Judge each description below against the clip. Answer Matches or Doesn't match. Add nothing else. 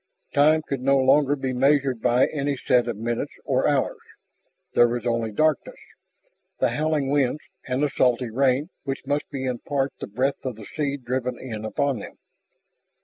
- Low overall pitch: Matches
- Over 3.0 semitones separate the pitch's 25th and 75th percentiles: Doesn't match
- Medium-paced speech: Matches